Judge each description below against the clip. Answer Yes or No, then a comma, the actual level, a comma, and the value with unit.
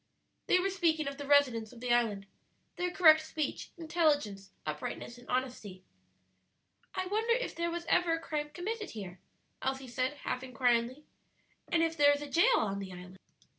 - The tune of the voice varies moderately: No, wide, 6.1 semitones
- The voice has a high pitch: Yes, very high, 285 Hz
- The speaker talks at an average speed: Yes, average, 170 wpm